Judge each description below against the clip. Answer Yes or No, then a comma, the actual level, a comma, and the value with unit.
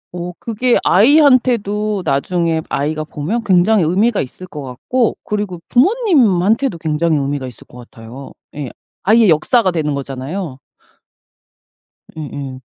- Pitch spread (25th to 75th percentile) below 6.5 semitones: No, wide, 7.3 semitones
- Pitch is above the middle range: No, medium, 175 Hz